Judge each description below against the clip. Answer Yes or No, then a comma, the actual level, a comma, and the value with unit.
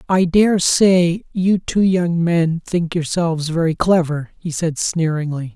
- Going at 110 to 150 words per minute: Yes, average, 140 wpm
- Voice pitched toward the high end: No, medium, 170 Hz